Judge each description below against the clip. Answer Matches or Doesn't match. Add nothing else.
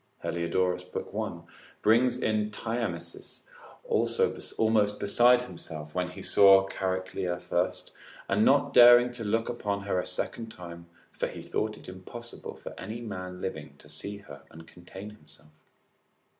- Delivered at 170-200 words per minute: Doesn't match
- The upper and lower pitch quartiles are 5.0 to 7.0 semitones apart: Doesn't match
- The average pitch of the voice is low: Matches